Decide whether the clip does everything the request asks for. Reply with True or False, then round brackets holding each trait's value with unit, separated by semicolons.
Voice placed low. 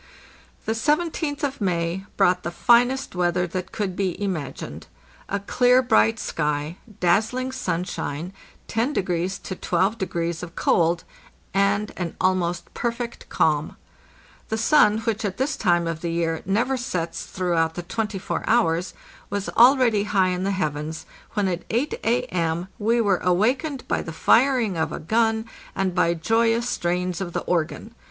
False (190 Hz)